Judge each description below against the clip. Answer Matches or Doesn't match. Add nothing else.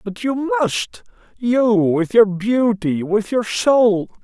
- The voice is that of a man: Matches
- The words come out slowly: Matches